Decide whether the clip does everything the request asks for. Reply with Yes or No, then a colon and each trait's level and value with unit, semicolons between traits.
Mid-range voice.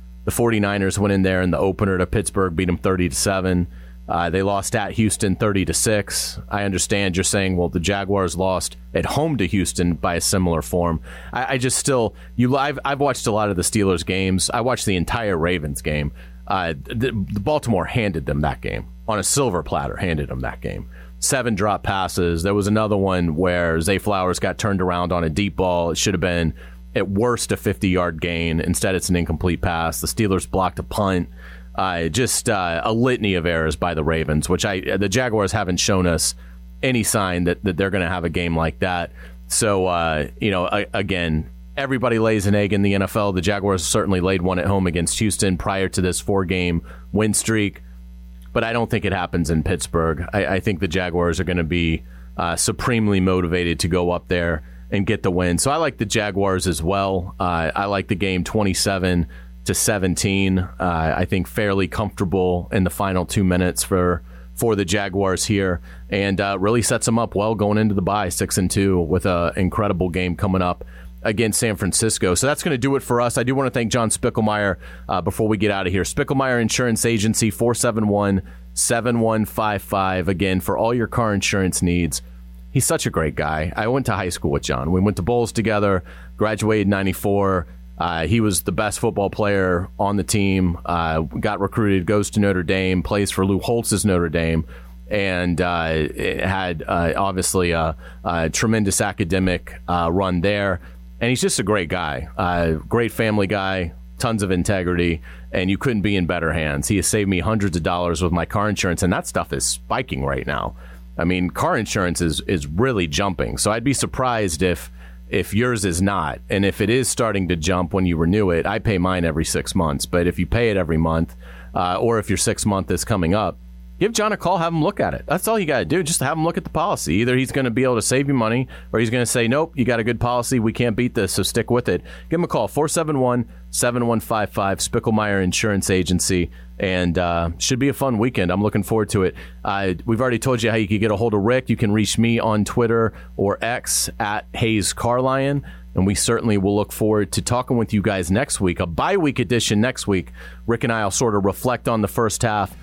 No: very low, 95 Hz